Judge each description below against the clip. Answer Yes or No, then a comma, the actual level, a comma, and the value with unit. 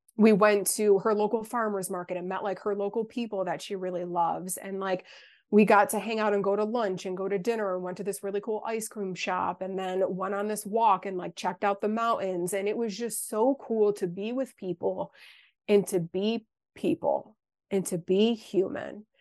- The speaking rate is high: Yes, fast, 220 wpm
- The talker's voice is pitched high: Yes, high, 200 Hz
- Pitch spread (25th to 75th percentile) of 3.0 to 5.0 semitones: No, narrow, 2.6 semitones